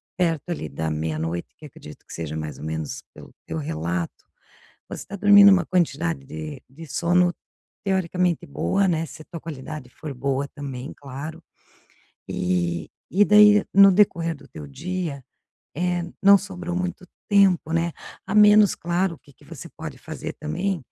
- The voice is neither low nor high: Yes, medium, 160 Hz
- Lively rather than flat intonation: Yes, wide, 6.4 semitones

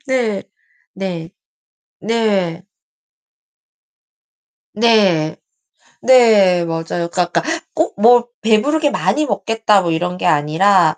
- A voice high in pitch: Yes, high, 195 Hz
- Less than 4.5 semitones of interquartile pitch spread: No, average, 4.8 semitones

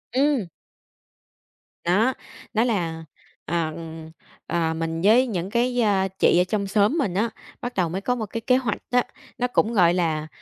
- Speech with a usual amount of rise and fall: No, wide, 6.0 semitones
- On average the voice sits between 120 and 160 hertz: No, high, 200 Hz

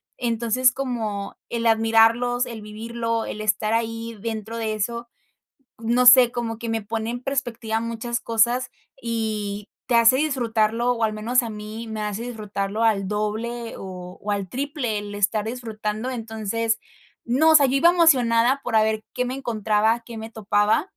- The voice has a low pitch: No, high, 230 Hz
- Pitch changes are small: Yes, narrow, 2.0 semitones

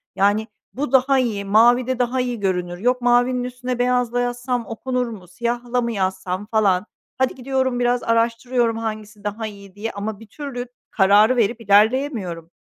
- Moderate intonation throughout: Yes, average, 3.3 semitones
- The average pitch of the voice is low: No, high, 235 Hz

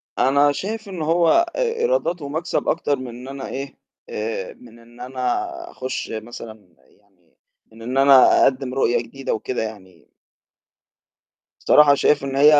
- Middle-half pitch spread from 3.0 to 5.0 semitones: Yes, average, 4.2 semitones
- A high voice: No, low, 135 Hz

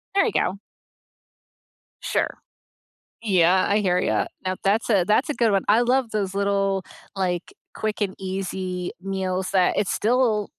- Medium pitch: No, high, 195 Hz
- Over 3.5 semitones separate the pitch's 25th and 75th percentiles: No, narrow, 2.5 semitones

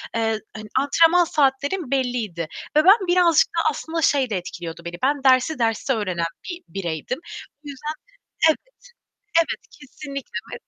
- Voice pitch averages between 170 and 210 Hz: No, very high, 270 Hz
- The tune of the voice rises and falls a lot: Yes, wide, 6.4 semitones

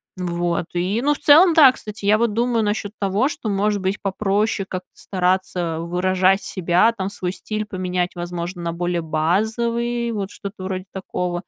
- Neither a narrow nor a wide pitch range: Yes, average, 3.2 semitones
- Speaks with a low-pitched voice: No, high, 190 Hz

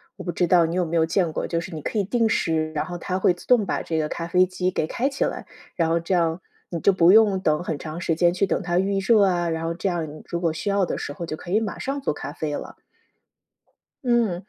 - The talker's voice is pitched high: No, medium, 175 Hz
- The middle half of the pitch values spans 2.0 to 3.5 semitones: Yes, average, 2.9 semitones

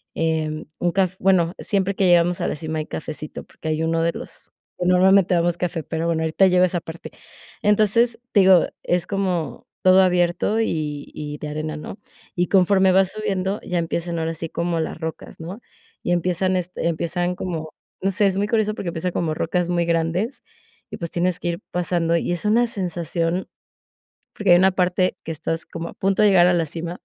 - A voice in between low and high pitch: Yes, medium, 175 Hz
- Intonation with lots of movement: No, narrow, 2.4 semitones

